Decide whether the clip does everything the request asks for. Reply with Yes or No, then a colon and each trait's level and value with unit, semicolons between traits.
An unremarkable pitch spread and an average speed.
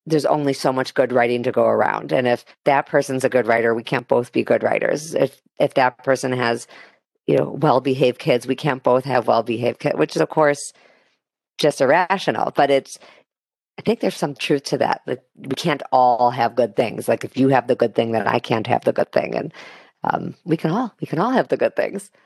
No: average, 3.2 semitones; fast, 230 wpm